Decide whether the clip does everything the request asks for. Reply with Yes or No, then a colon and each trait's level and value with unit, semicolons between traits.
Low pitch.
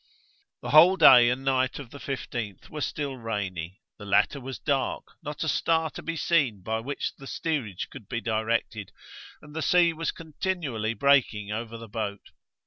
Yes: low, 130 Hz